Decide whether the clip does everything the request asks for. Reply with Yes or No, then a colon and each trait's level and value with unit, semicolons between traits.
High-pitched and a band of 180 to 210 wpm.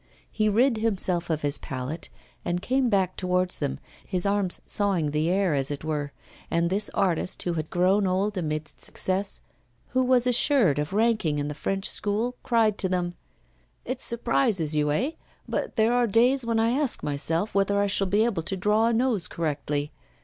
Yes: high, 195 Hz; average, 185 wpm